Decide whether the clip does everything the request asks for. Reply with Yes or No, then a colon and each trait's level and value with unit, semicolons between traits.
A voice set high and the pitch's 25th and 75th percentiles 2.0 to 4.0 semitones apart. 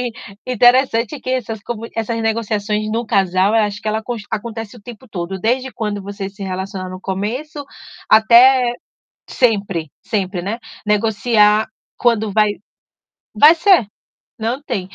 Yes: high, 220 Hz; average, 3.0 semitones